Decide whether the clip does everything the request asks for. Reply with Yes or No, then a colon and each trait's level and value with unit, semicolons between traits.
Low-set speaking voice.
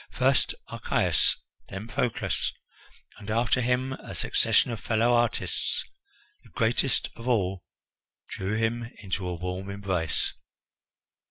Yes: low, 110 Hz